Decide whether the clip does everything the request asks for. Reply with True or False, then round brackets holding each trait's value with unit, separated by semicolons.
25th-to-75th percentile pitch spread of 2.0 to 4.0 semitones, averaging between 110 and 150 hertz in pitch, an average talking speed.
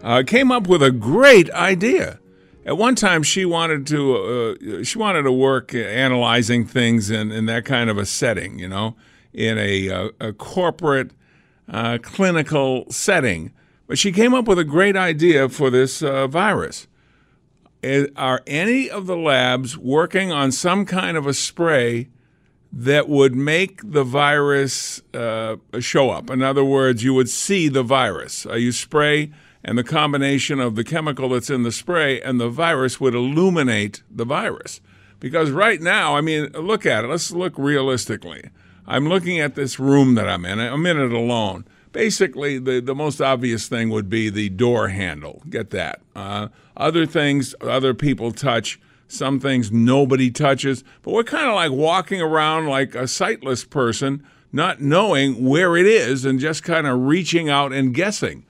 False (4.6 semitones; 135 Hz; 170 wpm)